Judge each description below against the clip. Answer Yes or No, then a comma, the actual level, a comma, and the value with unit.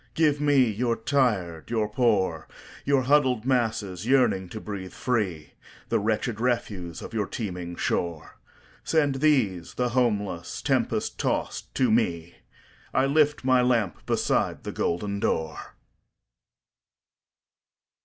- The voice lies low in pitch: Yes, low, 110 Hz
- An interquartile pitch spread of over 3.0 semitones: Yes, wide, 5.6 semitones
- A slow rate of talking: Yes, slow, 105 wpm